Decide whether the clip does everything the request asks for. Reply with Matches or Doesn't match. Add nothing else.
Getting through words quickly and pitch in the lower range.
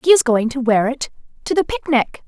Doesn't match